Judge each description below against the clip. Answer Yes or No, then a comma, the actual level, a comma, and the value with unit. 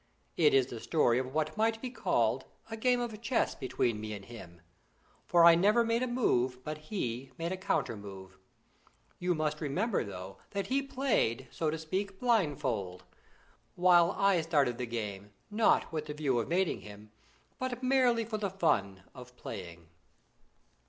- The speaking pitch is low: No, medium, 155 Hz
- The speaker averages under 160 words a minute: No, average, 170 wpm